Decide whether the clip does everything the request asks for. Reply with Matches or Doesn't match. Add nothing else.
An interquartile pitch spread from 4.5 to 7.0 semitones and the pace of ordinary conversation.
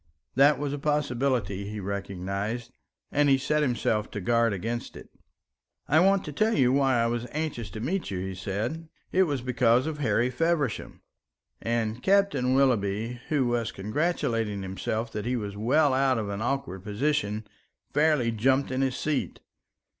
Matches